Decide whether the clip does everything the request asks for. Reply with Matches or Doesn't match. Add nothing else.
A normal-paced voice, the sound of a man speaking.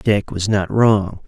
Matches